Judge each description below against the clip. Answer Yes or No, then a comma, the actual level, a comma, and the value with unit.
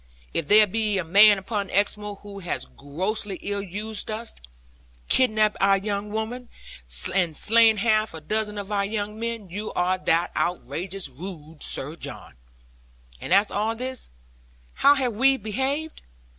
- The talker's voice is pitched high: Yes, high, 205 Hz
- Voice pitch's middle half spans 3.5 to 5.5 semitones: No, narrow, 2.5 semitones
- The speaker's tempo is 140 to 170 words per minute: Yes, average, 150 wpm